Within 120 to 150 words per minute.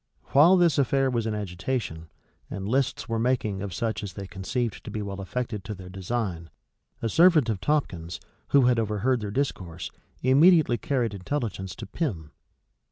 No: average, 165 wpm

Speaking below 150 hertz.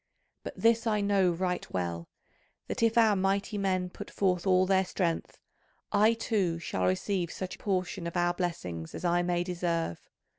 No: medium, 180 Hz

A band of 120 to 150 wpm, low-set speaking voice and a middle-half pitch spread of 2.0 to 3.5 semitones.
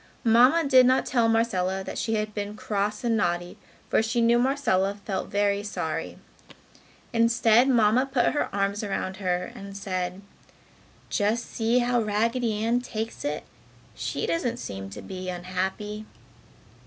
No: average, 145 wpm; high, 215 Hz; average, 3.2 semitones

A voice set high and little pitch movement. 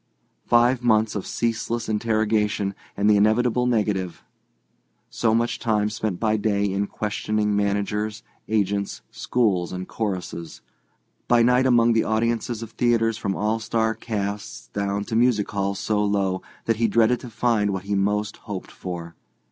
No: low, 105 Hz; narrow, 2.2 semitones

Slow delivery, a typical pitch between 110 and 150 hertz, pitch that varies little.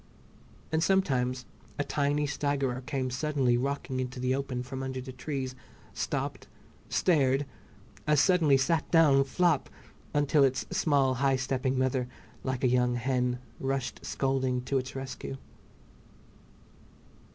Yes: slow, 130 wpm; low, 135 Hz; narrow, 1.9 semitones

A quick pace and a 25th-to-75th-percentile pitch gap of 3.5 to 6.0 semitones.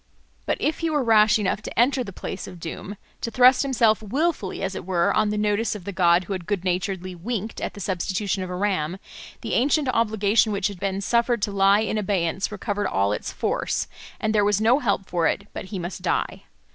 No: fast, 220 wpm; average, 3.0 semitones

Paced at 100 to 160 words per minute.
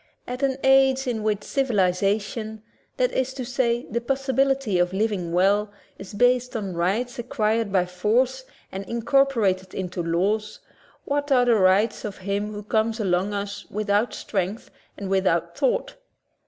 Yes: average, 155 wpm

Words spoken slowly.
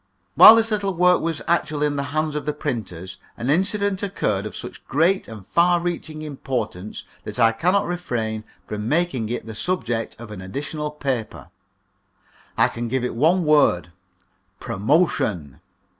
No: average, 160 wpm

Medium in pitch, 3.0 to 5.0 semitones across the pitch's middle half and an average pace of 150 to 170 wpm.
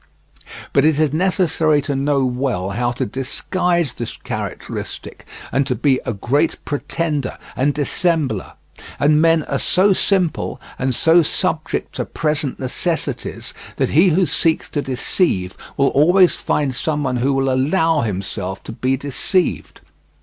No: medium, 145 Hz; average, 4.0 semitones; average, 140 wpm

